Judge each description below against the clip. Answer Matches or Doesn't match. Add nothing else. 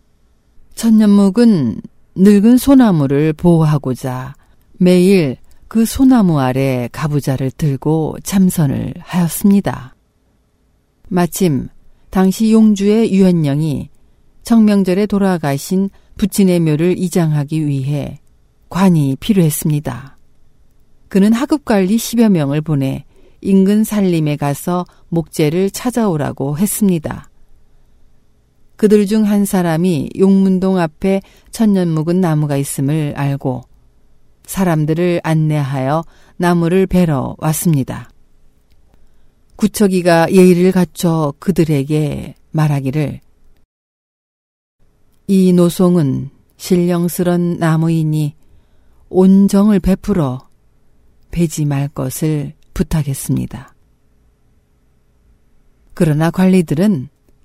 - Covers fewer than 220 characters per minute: Matches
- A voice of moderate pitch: Matches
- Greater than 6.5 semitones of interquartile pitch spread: Doesn't match